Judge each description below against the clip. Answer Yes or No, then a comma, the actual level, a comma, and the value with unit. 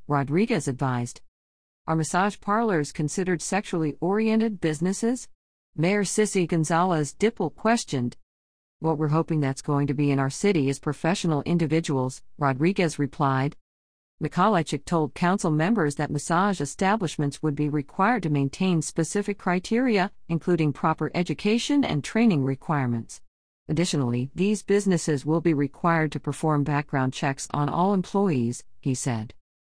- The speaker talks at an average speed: No, slow, 130 wpm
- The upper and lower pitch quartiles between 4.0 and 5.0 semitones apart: Yes, average, 4.6 semitones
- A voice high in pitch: No, medium, 155 Hz